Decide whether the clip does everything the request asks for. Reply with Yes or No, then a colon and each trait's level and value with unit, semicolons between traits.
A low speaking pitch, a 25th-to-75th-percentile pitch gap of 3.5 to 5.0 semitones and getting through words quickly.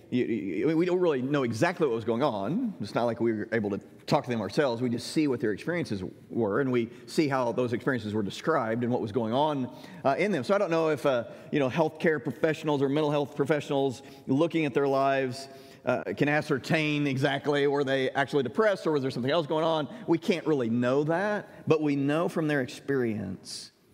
No: medium, 145 Hz; average, 3.8 semitones; fast, 225 wpm